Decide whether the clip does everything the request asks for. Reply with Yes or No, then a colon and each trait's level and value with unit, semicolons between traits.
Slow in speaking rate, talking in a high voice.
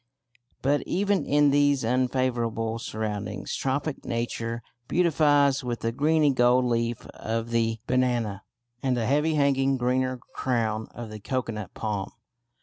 No: slow, 130 wpm; low, 125 Hz